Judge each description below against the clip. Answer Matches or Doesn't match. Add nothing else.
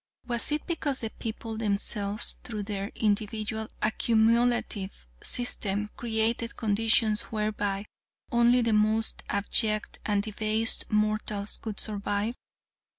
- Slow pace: Matches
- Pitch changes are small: Matches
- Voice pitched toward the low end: Doesn't match